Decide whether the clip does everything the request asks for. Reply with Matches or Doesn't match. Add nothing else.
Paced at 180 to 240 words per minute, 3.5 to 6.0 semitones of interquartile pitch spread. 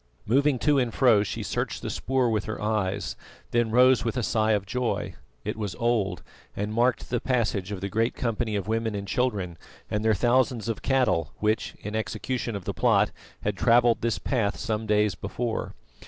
Doesn't match